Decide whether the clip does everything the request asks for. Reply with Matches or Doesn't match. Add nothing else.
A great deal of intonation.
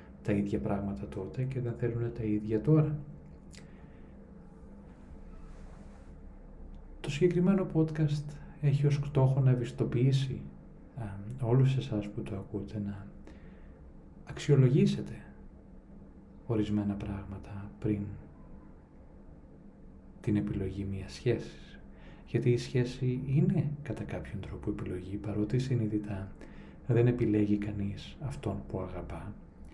Doesn't match